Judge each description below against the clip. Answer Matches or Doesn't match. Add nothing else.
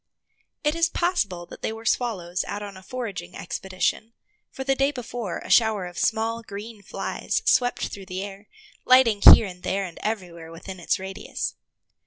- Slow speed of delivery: Doesn't match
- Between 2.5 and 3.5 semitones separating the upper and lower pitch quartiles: Doesn't match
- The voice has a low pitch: Doesn't match